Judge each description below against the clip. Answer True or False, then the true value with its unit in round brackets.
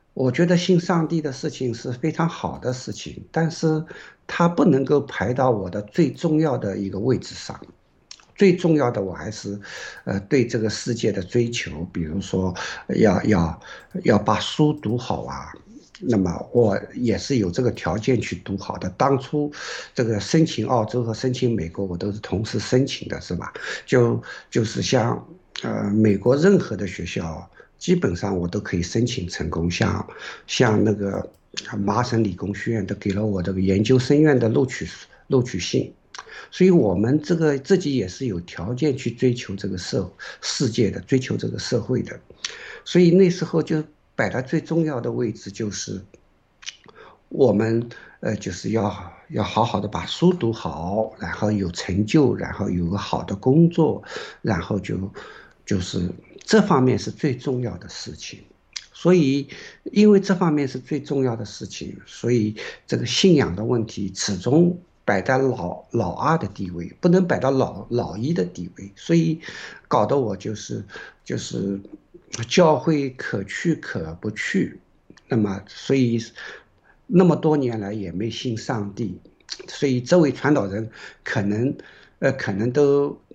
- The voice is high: False (115 Hz)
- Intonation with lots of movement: True (6.4 semitones)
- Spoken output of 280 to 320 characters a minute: False (230 characters per minute)